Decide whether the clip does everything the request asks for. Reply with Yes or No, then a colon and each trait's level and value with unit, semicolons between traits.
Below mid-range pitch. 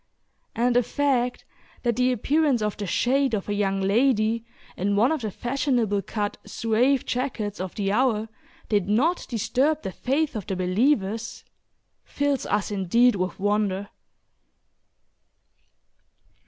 No: high, 225 Hz